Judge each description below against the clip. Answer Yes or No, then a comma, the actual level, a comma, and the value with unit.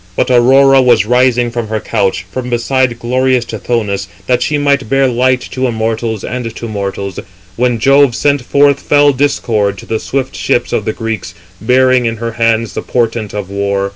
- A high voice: No, low, 120 Hz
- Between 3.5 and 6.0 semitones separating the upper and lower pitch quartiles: No, average, 2.8 semitones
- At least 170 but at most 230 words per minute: Yes, average, 180 wpm